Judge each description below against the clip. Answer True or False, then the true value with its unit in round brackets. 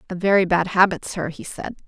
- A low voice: False (185 Hz)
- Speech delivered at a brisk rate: True (225 wpm)